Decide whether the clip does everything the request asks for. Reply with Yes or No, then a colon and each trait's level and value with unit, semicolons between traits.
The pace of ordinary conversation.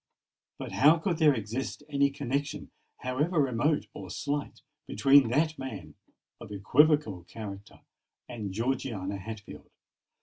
No: slow, 115 wpm